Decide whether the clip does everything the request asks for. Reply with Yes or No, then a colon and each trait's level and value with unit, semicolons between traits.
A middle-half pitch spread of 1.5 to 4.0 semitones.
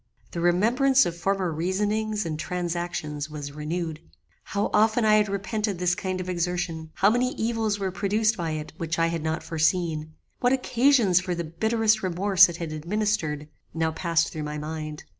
No: average, 4.7 semitones